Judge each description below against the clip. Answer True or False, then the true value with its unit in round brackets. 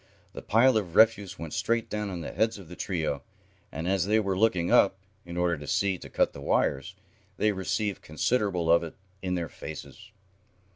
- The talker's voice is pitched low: True (95 Hz)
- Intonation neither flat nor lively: True (4.0 semitones)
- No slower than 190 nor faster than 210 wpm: True (195 wpm)